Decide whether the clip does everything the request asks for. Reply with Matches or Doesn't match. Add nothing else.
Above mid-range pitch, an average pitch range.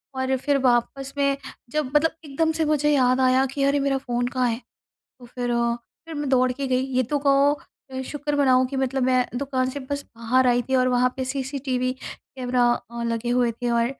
Doesn't match